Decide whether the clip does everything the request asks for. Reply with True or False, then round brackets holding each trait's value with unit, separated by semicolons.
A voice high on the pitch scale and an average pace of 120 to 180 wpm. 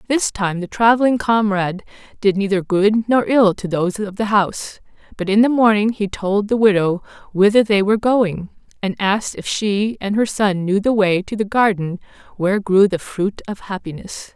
False (205 Hz; 190 wpm)